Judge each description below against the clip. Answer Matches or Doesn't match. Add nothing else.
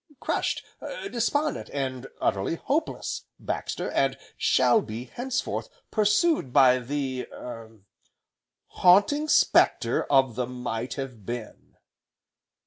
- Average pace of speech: Doesn't match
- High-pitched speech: Doesn't match